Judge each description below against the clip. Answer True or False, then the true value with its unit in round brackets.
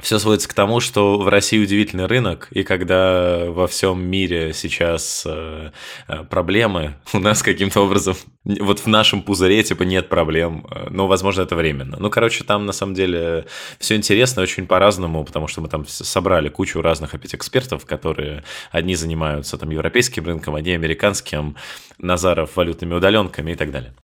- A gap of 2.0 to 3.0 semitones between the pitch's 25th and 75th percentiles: False (3.9 semitones)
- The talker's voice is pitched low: True (90 Hz)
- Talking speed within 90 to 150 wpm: False (160 wpm)